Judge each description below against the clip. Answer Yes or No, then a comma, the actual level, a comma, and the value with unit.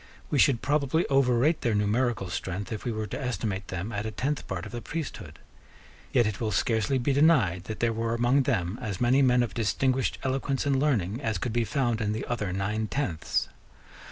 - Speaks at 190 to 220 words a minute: Yes, fast, 205 wpm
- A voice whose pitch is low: Yes, low, 115 Hz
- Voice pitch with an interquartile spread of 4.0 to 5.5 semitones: Yes, average, 4.3 semitones